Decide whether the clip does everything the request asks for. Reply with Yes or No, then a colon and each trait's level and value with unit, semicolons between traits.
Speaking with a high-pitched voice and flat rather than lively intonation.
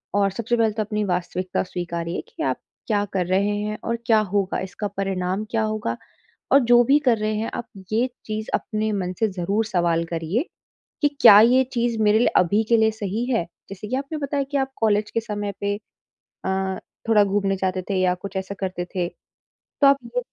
No: high, 210 Hz; average, 3.1 semitones